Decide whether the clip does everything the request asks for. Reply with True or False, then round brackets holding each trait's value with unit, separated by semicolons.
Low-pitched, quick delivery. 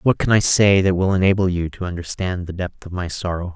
True (90 Hz; 255 wpm)